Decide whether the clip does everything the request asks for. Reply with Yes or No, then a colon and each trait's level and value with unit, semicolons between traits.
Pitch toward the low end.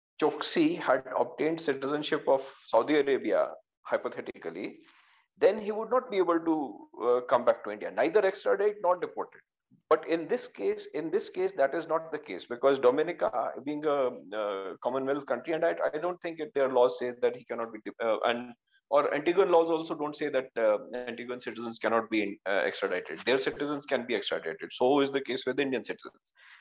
No: medium, 155 Hz